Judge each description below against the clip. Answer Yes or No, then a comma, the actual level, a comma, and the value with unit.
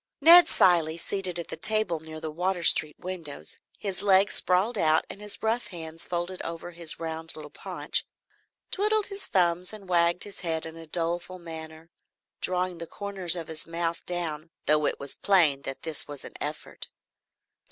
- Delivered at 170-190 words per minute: Yes, average, 175 wpm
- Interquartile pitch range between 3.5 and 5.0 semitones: No, average, 2.8 semitones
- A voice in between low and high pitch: Yes, medium, 170 Hz